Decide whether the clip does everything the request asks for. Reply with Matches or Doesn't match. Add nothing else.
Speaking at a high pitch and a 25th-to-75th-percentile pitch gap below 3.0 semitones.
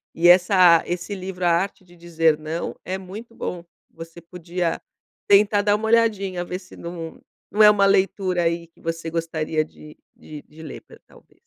Doesn't match